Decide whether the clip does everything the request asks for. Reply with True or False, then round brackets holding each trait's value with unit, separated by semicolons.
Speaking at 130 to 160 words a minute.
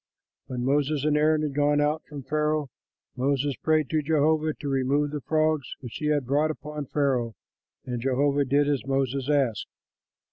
False (170 wpm)